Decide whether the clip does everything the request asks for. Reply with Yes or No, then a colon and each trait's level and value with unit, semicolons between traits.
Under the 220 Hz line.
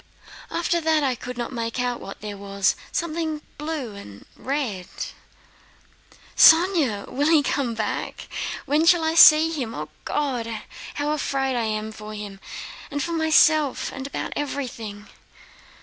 No: very high, 270 Hz